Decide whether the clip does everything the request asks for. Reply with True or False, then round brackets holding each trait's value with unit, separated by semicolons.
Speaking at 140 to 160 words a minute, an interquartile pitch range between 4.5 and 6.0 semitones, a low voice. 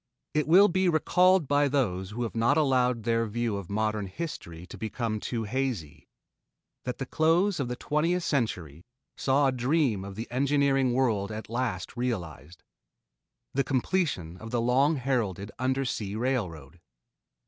True (150 wpm; 4.9 semitones; 125 Hz)